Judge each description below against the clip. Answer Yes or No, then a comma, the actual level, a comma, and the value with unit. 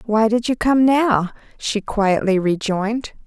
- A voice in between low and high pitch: No, high, 220 Hz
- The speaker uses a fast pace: No, average, 145 wpm